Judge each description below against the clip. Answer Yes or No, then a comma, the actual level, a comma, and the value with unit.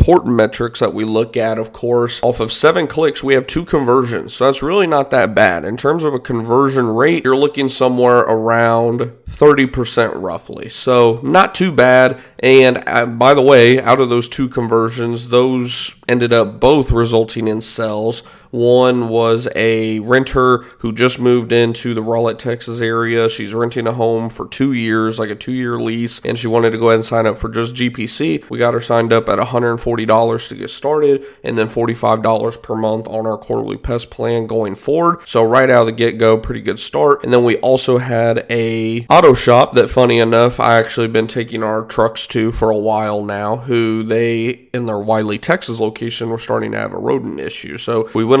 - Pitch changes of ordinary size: No, narrow, 1.8 semitones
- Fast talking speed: No, average, 195 wpm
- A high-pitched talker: No, low, 115 Hz